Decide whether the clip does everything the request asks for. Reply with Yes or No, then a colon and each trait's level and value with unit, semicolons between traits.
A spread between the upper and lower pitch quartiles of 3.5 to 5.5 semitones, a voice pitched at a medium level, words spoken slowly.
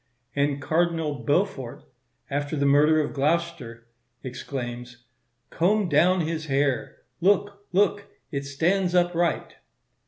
Yes: average, 4.1 semitones; medium, 155 Hz; slow, 105 wpm